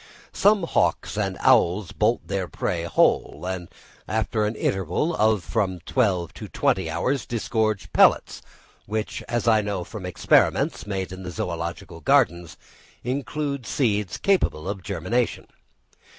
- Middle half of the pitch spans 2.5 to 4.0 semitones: No, average, 4.4 semitones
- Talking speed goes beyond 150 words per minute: No, slow, 135 wpm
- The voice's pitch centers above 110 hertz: No, low, 100 Hz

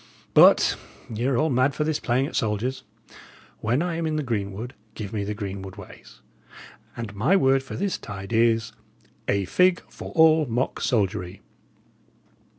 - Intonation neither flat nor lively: No, wide, 6.2 semitones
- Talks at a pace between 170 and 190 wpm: No, average, 155 wpm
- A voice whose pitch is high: No, low, 120 Hz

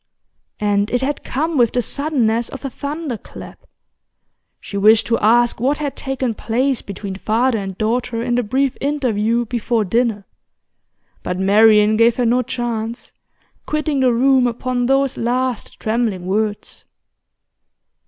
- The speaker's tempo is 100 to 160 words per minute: Yes, average, 140 wpm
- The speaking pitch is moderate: No, high, 240 Hz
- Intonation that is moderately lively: Yes, average, 3.1 semitones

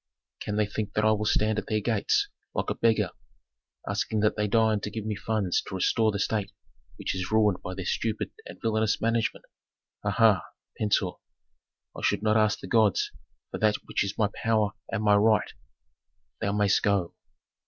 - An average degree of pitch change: No, narrow, 1.3 semitones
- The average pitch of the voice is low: Yes, low, 105 Hz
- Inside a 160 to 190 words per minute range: Yes, average, 185 wpm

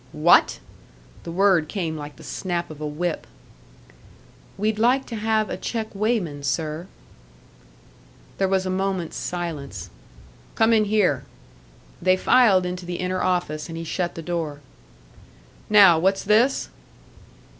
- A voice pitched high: No, medium, 180 Hz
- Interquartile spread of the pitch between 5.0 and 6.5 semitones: No, average, 4.3 semitones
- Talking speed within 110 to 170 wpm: Yes, slow, 135 wpm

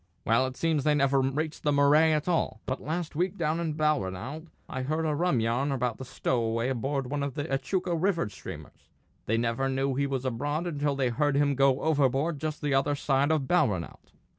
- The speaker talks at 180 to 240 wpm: Yes, fast, 205 wpm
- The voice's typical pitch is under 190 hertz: Yes, medium, 140 Hz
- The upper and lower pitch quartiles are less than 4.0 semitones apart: Yes, average, 2.9 semitones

